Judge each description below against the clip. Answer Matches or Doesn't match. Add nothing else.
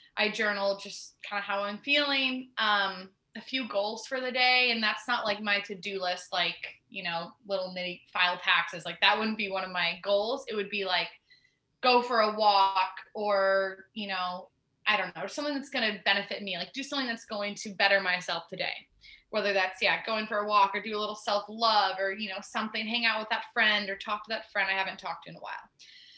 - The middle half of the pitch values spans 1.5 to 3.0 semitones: Matches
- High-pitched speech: Matches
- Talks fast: Matches